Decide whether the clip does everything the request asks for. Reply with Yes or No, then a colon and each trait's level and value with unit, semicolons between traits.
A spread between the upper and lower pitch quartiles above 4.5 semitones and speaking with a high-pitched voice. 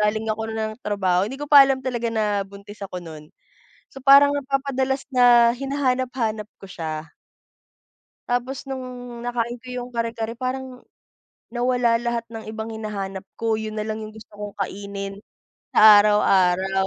No: average, 3.6 semitones; high, 225 Hz